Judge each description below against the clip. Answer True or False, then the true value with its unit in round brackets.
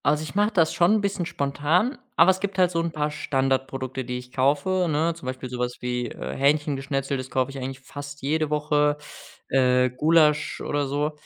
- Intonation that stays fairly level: False (3.4 semitones)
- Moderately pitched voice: True (145 Hz)